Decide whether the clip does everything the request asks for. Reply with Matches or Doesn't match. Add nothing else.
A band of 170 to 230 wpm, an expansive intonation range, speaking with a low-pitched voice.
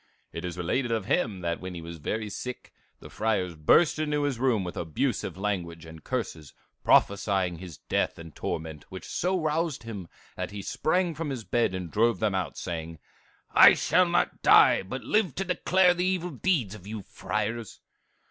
Matches